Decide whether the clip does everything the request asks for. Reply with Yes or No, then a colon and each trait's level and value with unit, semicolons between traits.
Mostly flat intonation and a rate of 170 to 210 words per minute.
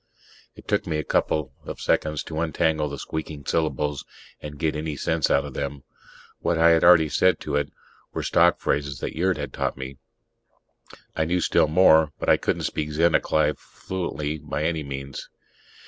Yes: narrow, 1.9 semitones; average, 180 wpm